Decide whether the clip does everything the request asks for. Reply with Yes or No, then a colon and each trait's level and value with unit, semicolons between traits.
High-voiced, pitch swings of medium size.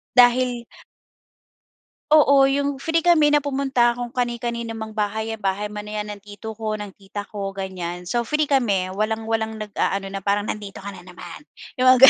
Yes: high, 220 Hz; average, 3.8 semitones